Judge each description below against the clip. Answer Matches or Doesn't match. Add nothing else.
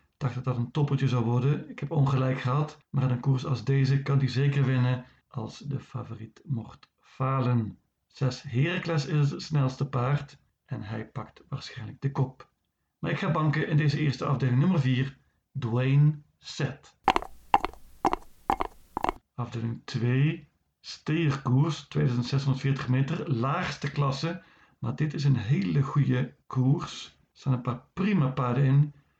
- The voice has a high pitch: Doesn't match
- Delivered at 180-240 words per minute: Doesn't match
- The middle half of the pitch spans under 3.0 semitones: Matches